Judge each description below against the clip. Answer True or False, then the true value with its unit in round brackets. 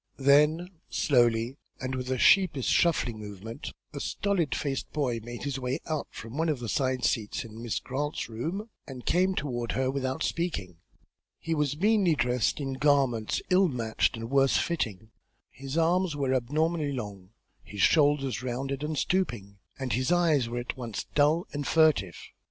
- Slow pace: False (165 wpm)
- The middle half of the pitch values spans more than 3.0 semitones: True (4.5 semitones)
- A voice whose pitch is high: False (135 Hz)